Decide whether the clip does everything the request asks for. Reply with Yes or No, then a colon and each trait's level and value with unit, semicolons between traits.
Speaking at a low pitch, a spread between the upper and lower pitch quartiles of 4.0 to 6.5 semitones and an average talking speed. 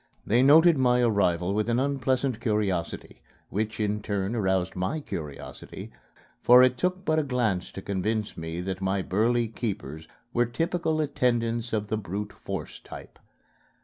Yes: low, 110 Hz; average, 4.7 semitones; average, 150 wpm